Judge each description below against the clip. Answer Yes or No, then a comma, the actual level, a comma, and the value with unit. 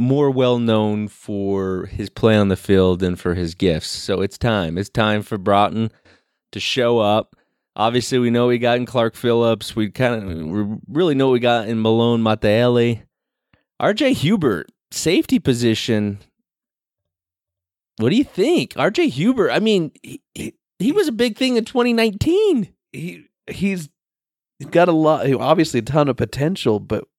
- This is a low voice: Yes, low, 120 Hz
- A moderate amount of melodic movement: No, wide, 6.8 semitones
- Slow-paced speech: No, average, 170 wpm